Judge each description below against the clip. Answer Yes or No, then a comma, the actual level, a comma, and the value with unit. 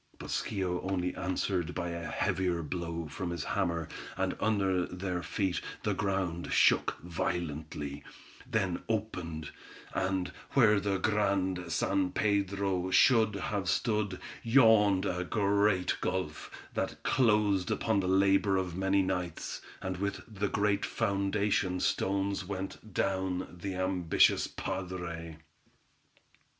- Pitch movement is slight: Yes, narrow, 2.1 semitones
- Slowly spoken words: Yes, slow, 120 wpm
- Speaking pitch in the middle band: No, very low, 95 Hz